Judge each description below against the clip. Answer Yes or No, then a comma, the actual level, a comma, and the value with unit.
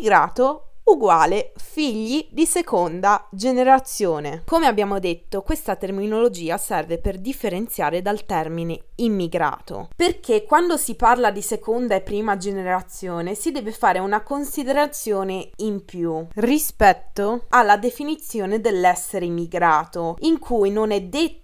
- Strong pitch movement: Yes, wide, 6.7 semitones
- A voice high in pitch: Yes, high, 215 Hz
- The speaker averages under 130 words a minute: Yes, average, 120 wpm